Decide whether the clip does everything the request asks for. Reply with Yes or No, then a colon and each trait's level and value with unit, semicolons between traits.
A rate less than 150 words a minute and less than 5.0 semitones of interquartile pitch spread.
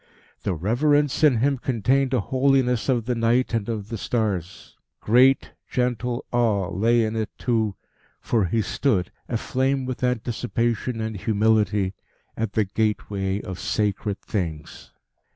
Yes: slow, 135 wpm; average, 3.3 semitones